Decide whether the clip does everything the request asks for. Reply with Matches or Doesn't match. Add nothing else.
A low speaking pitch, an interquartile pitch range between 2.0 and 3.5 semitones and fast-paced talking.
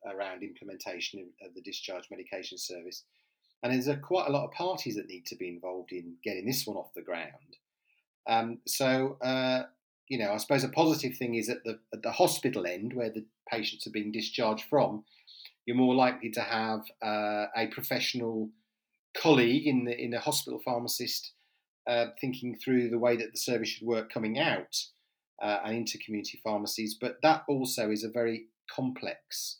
Doesn't match